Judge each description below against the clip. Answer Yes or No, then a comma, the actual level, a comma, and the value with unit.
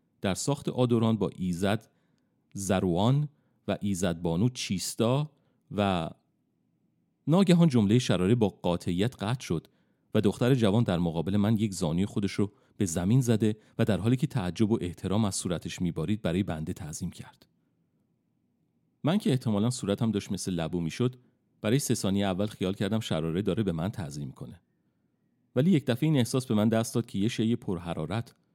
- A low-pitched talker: Yes, low, 110 Hz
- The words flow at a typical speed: No, fast, 165 wpm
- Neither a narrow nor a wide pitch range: Yes, average, 4.4 semitones